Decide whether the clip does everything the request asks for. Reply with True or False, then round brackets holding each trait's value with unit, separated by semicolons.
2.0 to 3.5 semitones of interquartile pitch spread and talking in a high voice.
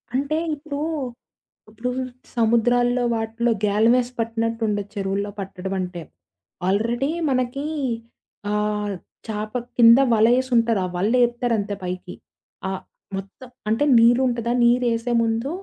True (2.8 semitones; 230 Hz)